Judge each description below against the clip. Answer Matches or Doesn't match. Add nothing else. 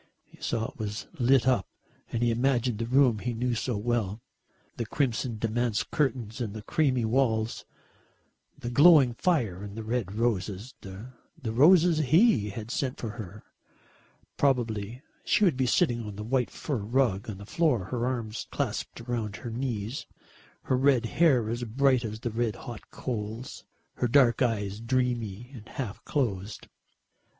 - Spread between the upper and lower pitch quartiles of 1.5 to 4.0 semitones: Matches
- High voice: Doesn't match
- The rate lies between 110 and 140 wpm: Doesn't match